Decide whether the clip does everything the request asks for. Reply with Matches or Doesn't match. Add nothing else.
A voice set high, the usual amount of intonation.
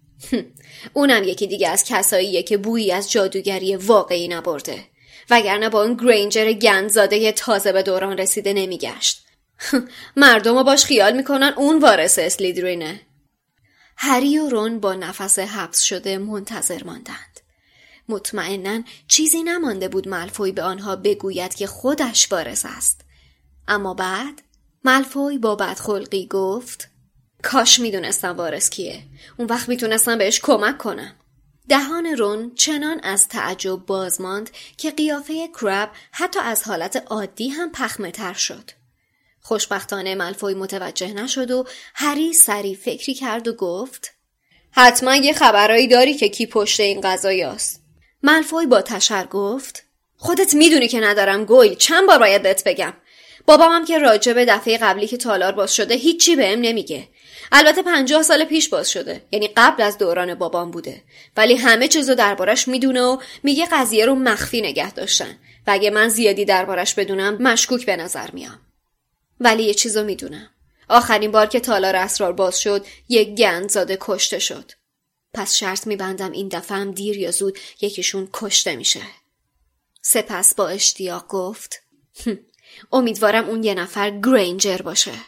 Matches